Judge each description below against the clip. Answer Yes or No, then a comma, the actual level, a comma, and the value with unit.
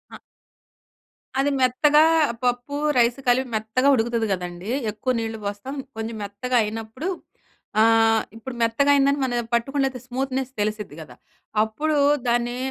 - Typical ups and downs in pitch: Yes, average, 3.1 semitones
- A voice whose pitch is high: Yes, high, 240 Hz